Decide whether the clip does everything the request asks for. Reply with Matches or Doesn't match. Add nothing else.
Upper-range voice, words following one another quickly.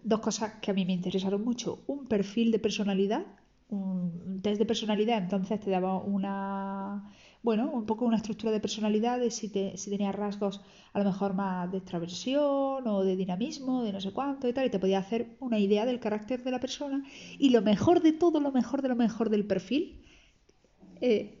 Matches